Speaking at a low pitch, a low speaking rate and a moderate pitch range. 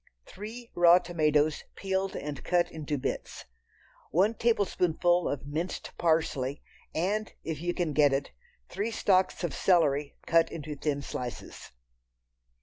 No: medium, 165 Hz; slow, 130 wpm; average, 3.8 semitones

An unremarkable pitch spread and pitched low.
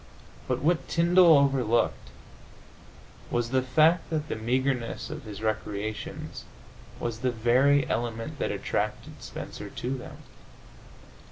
Yes: average, 3.9 semitones; low, 125 Hz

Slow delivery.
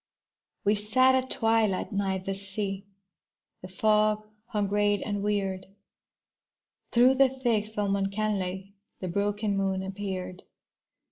Yes: slow, 120 wpm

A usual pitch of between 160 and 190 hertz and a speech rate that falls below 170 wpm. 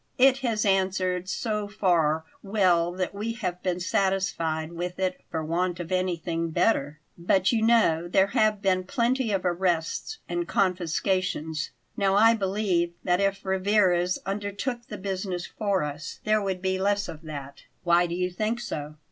Yes: medium, 185 Hz; average, 160 wpm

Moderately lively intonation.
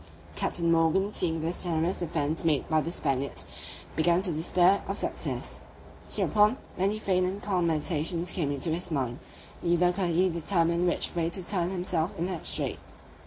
No: narrow, 2.2 semitones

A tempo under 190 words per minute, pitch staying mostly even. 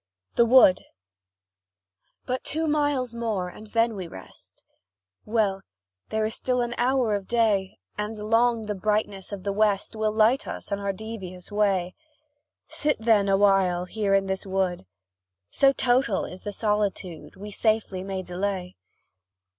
No: average, 145 wpm; average, 3.0 semitones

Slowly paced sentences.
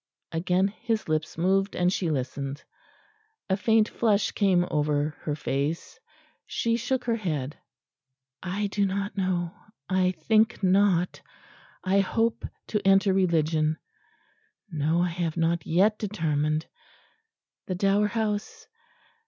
Yes: slow, 120 wpm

